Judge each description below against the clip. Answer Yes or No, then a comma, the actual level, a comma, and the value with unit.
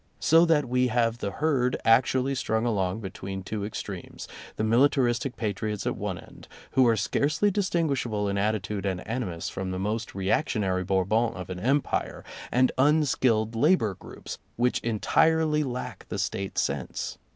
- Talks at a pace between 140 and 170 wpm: Yes, average, 155 wpm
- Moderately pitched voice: No, low, 115 Hz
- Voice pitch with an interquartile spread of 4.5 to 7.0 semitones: Yes, average, 5.0 semitones